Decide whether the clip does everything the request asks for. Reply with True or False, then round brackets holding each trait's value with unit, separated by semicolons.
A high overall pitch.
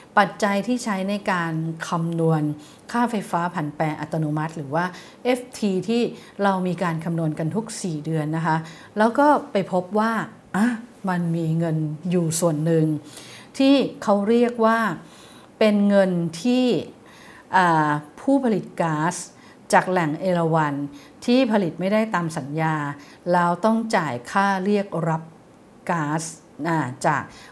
False (180 Hz)